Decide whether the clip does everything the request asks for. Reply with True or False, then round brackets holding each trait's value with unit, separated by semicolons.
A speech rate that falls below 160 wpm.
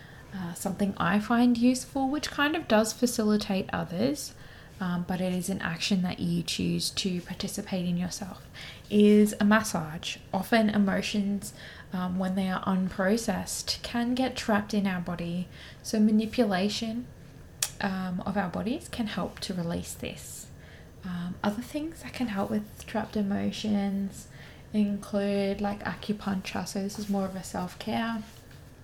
True (150 wpm)